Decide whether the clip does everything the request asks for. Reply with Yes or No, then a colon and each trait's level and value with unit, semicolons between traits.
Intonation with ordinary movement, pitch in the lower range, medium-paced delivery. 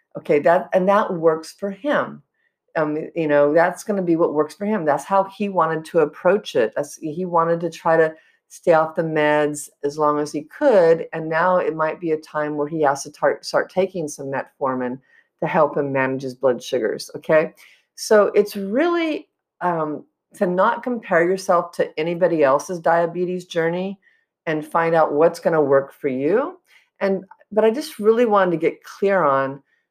No: average, 4.6 semitones; medium, 170 Hz; average, 195 wpm